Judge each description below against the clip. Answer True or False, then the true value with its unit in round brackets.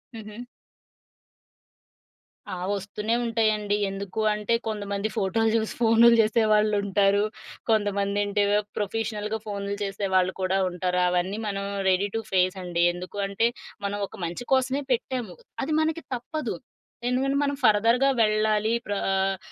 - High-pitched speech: True (210 Hz)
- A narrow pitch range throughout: True (2.2 semitones)